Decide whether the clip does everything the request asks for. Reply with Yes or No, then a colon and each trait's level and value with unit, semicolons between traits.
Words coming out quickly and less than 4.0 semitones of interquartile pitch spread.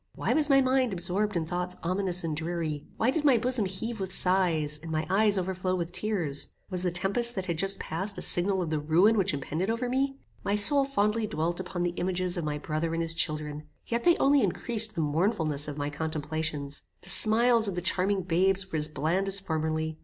No: fast, 215 wpm; average, 4.8 semitones